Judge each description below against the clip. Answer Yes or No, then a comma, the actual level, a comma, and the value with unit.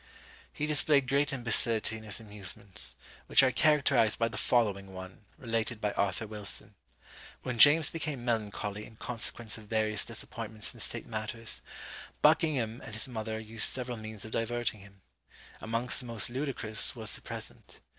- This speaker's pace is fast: No, average, 160 wpm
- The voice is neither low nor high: No, low, 115 Hz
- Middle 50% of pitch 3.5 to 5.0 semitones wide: No, narrow, 2.5 semitones